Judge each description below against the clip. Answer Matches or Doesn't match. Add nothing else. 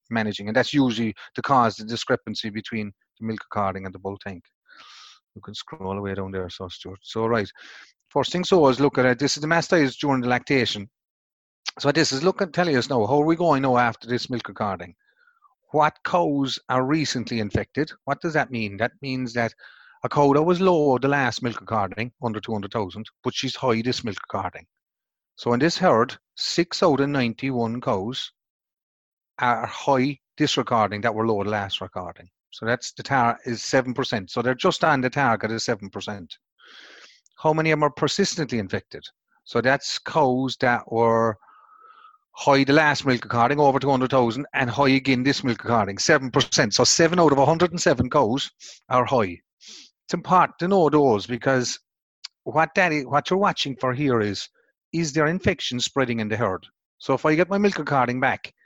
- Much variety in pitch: Doesn't match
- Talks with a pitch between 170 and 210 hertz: Doesn't match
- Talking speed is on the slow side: Doesn't match